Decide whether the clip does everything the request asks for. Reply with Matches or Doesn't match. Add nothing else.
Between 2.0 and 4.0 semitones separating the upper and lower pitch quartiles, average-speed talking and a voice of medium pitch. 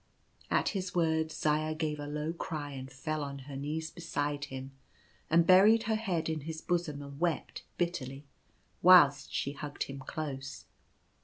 Matches